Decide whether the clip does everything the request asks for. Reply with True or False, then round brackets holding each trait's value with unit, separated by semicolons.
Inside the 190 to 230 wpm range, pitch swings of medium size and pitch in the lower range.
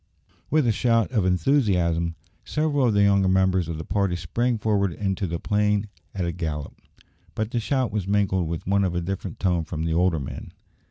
True (200 wpm; 3.8 semitones; 95 Hz)